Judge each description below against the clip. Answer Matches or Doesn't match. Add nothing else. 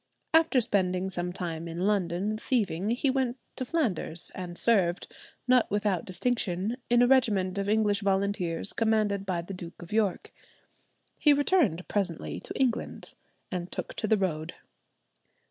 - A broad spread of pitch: Doesn't match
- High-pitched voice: Matches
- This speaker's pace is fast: Doesn't match